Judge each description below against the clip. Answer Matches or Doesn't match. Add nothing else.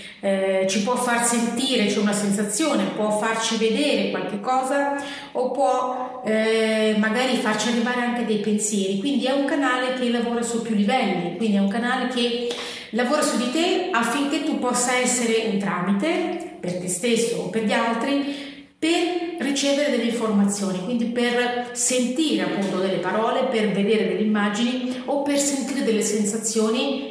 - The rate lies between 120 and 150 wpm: Doesn't match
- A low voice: Doesn't match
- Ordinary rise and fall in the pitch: Matches